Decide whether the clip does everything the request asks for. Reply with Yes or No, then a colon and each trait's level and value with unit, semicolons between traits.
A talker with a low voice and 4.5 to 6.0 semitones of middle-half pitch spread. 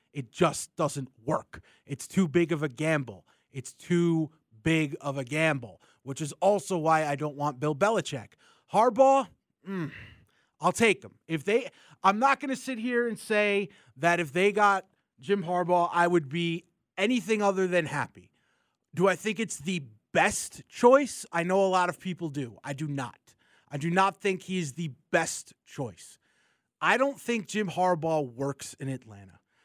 No: medium, 170 Hz; average, 5.1 semitones